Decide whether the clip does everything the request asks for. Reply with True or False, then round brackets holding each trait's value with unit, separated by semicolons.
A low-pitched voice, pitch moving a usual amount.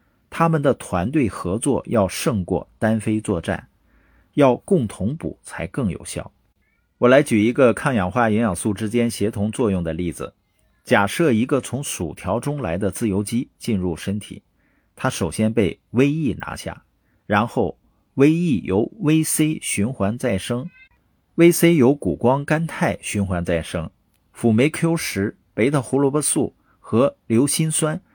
False (120 Hz; 6.8 semitones)